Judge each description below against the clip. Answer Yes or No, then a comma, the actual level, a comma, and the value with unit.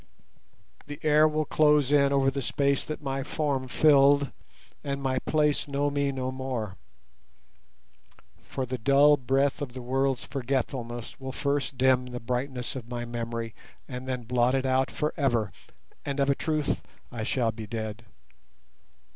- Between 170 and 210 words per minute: No, average, 155 wpm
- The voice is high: No, low, 135 Hz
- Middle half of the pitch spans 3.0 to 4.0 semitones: No, narrow, 2.4 semitones